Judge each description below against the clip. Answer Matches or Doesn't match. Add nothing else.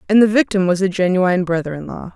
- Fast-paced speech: Matches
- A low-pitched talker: Doesn't match